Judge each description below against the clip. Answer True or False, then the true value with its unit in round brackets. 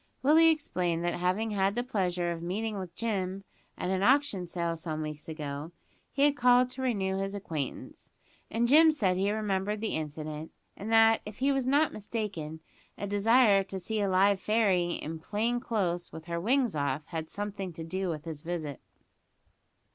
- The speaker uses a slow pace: False (180 wpm)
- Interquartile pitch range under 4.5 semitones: False (4.8 semitones)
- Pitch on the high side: True (195 Hz)